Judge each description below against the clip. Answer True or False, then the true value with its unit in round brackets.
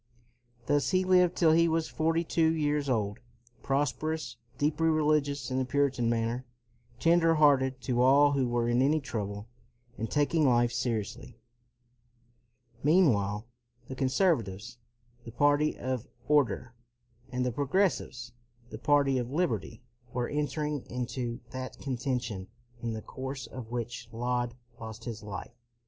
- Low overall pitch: True (130 Hz)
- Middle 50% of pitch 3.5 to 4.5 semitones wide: True (3.9 semitones)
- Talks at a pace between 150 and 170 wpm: False (140 wpm)